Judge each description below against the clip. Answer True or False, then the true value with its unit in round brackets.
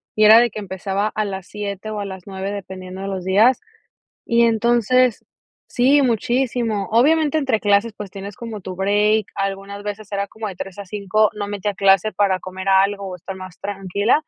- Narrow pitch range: True (2.2 semitones)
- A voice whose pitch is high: True (205 Hz)